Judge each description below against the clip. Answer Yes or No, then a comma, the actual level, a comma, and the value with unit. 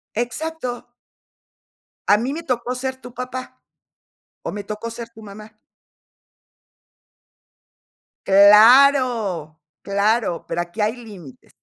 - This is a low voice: No, high, 230 Hz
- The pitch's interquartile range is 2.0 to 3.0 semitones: No, average, 3.7 semitones